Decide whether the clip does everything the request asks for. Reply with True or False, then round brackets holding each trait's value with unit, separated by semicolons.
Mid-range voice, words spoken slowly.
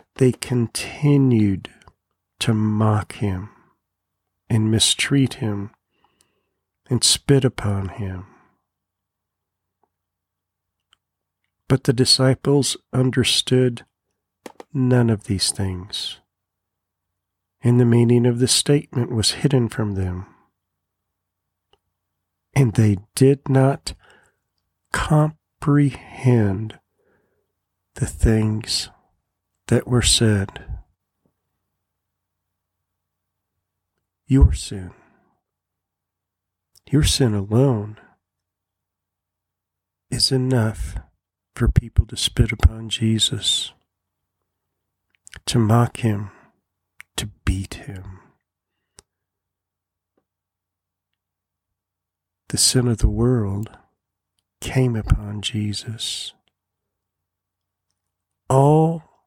False (100 Hz; 70 wpm)